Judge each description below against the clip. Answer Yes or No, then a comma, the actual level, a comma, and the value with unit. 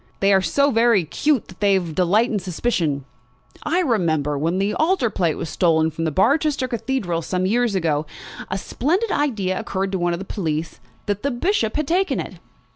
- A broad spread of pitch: Yes, wide, 6.6 semitones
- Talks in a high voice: Yes, high, 195 Hz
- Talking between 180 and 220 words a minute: Yes, average, 185 wpm